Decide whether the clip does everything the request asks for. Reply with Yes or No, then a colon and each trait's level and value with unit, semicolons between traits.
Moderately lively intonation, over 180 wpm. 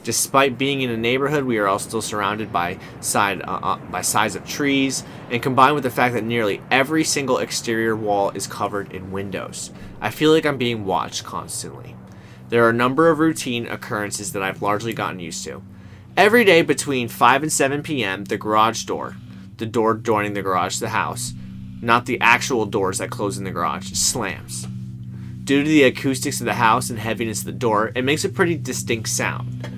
No: wide, 5.7 semitones; average, 200 wpm